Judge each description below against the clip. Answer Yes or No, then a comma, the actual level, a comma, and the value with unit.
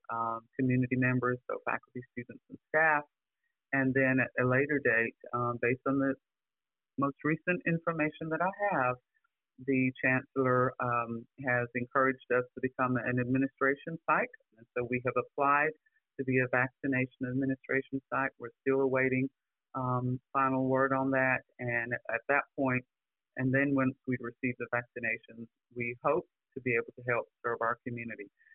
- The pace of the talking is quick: No, average, 160 wpm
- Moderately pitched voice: No, low, 130 Hz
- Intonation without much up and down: Yes, narrow, 1.7 semitones